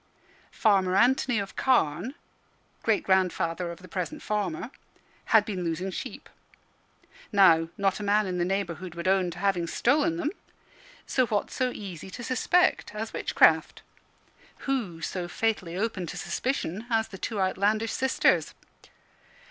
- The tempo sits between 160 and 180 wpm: No, average, 140 wpm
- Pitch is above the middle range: Yes, high, 195 Hz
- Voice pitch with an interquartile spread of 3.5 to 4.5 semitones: Yes, average, 4.0 semitones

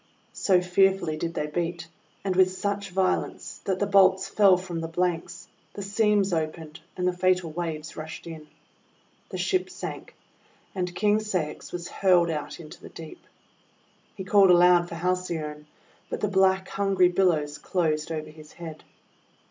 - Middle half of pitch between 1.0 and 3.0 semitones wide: Yes, average, 2.7 semitones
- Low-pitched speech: No, medium, 180 Hz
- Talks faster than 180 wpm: No, average, 165 wpm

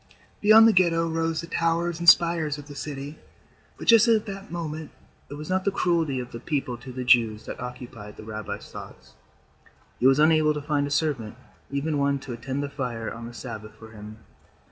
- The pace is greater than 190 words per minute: Yes, fast, 205 wpm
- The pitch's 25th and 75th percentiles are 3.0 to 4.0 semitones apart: No, average, 5.2 semitones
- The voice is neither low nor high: Yes, medium, 145 Hz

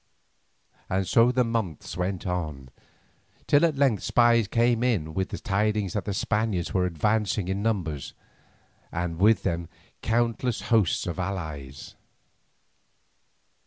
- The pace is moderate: No, slow, 125 wpm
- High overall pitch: No, low, 100 Hz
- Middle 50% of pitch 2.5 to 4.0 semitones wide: No, average, 4.7 semitones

